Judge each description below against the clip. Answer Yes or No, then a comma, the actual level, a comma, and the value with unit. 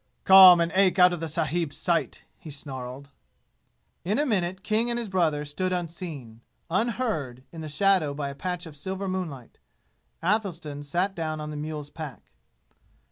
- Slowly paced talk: No, average, 165 wpm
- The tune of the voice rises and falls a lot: No, average, 4.3 semitones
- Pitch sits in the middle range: Yes, medium, 170 Hz